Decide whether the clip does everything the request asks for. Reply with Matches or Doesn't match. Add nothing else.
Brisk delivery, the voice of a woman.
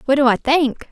Matches